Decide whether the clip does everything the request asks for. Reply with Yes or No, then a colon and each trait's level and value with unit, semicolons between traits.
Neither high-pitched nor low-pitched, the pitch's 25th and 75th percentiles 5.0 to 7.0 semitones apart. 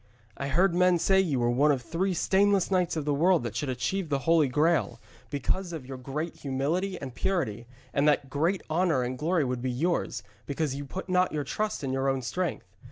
Yes: medium, 150 Hz; average, 5.3 semitones